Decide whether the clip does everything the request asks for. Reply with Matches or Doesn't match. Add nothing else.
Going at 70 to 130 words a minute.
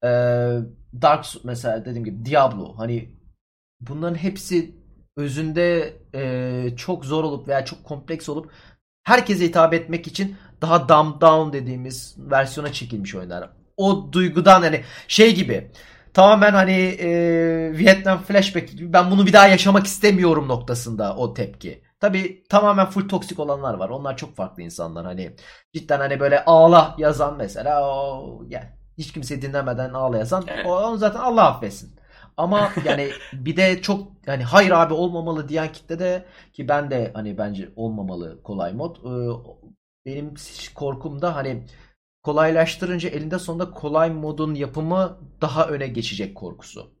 Doesn't match